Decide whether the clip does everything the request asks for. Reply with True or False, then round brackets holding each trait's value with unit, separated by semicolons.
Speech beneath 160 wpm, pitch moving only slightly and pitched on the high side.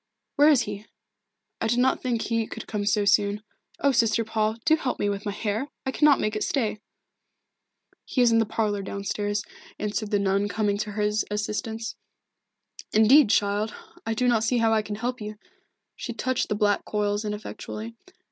False (185 wpm; 1.9 semitones; 215 Hz)